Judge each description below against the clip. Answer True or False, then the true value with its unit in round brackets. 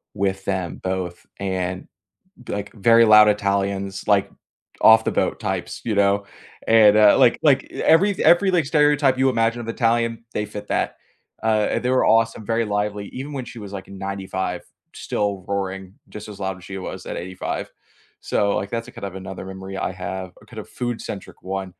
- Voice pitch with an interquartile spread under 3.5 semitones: True (3.1 semitones)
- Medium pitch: False (100 Hz)